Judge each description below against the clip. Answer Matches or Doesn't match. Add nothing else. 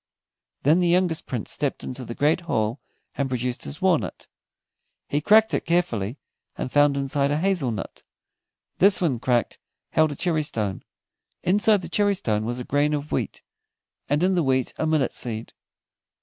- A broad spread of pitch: Matches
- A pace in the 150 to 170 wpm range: Matches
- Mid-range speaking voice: Matches